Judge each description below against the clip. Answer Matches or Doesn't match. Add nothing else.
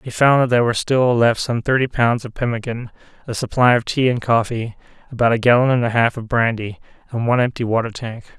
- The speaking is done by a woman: Doesn't match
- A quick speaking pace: Matches